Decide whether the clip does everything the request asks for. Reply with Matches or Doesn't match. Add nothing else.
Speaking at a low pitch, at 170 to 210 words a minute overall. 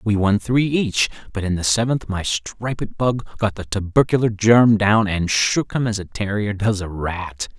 Matches